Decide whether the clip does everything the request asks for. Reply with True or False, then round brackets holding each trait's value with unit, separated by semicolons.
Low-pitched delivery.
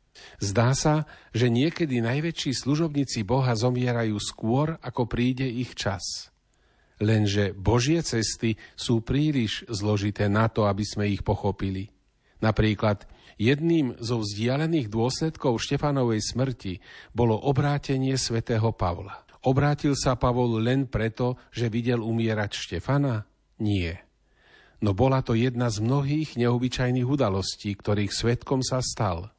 True (120 Hz)